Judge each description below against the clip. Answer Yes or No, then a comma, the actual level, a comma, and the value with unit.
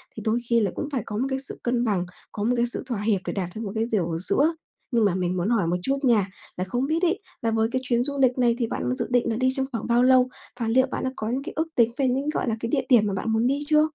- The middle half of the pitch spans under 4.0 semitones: Yes, average, 3.4 semitones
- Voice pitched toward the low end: No, high, 235 Hz